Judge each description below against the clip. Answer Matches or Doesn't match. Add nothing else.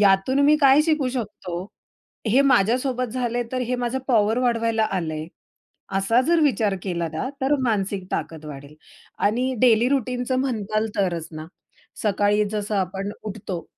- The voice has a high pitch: Matches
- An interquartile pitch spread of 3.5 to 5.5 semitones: Matches